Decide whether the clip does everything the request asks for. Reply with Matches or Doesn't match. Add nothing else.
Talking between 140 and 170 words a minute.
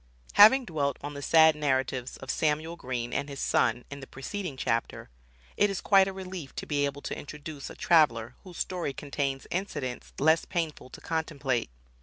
Doesn't match